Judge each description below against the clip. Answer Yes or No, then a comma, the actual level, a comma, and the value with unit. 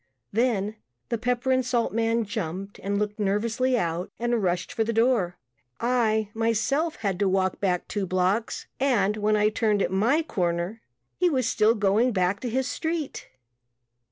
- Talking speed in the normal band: Yes, average, 165 wpm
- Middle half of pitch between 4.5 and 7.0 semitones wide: No, average, 3.5 semitones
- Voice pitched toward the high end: Yes, high, 215 Hz